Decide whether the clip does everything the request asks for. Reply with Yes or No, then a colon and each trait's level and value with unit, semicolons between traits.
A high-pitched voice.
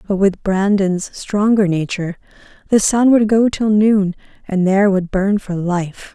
Yes: high, 200 Hz